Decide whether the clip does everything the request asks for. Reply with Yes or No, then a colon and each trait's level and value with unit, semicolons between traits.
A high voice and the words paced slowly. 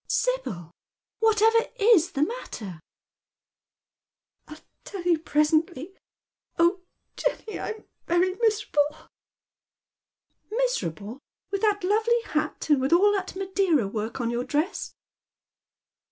Yes: very high, 350 Hz; slow, 120 wpm